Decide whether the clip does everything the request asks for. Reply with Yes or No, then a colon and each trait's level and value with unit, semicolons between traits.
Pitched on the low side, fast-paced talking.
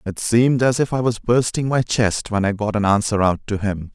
Yes: low, 110 Hz; fast, 260 wpm